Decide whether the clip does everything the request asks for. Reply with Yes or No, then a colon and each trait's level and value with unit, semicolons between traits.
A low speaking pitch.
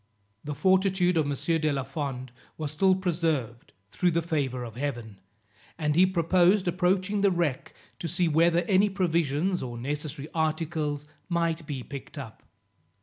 No: medium, 160 Hz